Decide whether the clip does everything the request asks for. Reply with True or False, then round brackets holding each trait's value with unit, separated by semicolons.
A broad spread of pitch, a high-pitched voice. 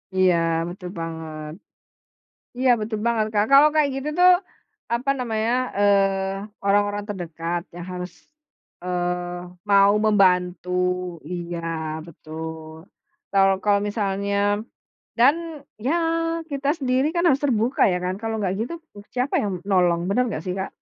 False (4.2 semitones; 200 Hz)